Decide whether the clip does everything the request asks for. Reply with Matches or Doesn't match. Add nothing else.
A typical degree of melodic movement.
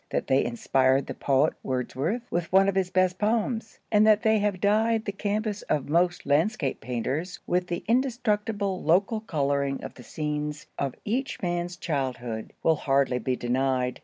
Doesn't match